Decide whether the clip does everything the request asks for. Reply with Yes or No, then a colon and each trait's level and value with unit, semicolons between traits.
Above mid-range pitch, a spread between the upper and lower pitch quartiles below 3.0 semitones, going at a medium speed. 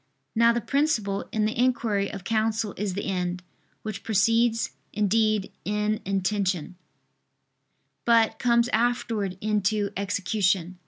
No: high, 210 Hz; narrow, 2.6 semitones; slow, 115 wpm